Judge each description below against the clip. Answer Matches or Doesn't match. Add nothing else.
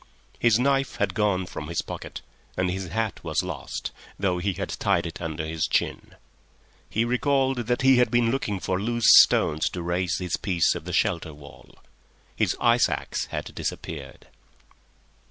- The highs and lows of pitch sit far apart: Matches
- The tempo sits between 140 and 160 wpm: Doesn't match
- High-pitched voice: Doesn't match